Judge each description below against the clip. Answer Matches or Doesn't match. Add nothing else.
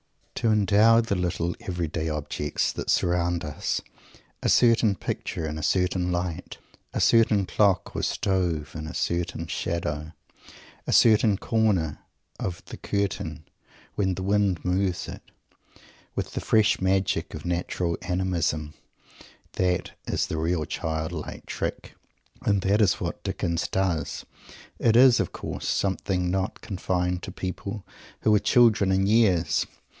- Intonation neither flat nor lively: Matches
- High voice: Doesn't match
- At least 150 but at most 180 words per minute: Doesn't match